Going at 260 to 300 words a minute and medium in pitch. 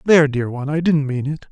Yes: fast, 275 wpm; medium, 145 Hz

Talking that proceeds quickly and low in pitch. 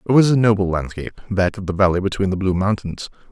Yes: fast, 235 wpm; low, 100 Hz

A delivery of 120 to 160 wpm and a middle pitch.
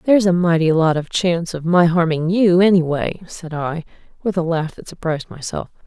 No: average, 195 wpm; medium, 170 Hz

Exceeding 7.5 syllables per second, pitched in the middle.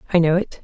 Yes: 8.1 syllables/s; medium, 170 Hz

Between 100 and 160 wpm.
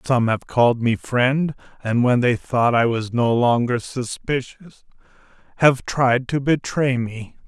Yes: average, 155 wpm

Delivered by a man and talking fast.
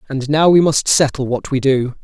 Yes: male; fast, 235 wpm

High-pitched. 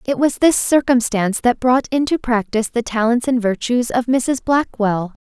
Yes: high, 240 Hz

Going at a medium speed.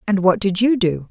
No: fast, 270 wpm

